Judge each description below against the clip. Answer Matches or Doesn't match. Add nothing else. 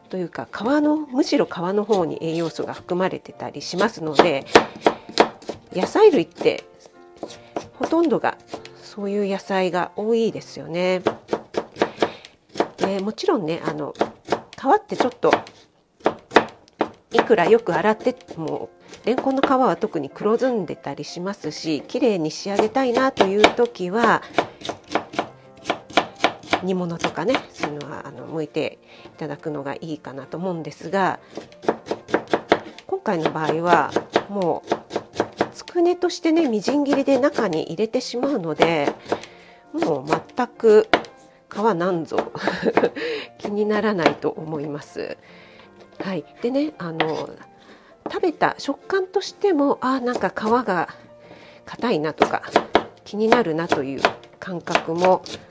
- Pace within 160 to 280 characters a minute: Matches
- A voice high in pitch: Matches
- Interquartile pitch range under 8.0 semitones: Doesn't match